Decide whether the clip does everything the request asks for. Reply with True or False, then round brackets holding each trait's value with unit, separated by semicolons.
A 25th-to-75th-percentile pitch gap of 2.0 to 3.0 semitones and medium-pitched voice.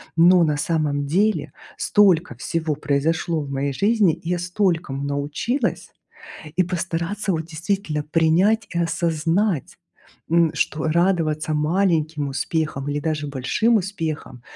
False (3.4 semitones; 160 Hz)